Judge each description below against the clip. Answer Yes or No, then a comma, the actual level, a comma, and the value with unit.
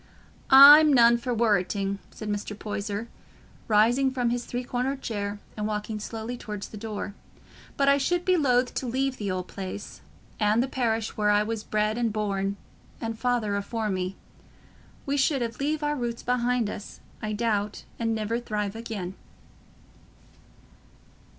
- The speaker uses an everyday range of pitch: Yes, average, 3.0 semitones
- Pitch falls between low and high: No, high, 225 Hz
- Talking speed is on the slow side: No, average, 155 wpm